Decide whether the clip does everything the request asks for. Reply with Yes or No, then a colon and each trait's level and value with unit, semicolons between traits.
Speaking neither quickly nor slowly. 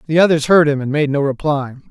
No: fast, 250 wpm